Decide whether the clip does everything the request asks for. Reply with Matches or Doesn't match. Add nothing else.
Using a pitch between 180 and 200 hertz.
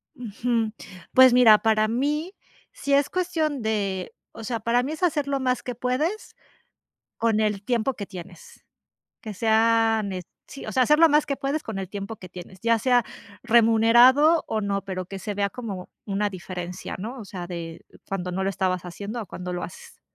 Doesn't match